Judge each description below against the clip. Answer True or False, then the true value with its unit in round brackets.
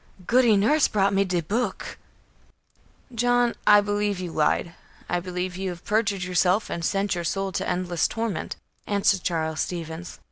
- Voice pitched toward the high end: True (195 Hz)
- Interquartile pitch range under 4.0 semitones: True (2.8 semitones)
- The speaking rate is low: False (155 wpm)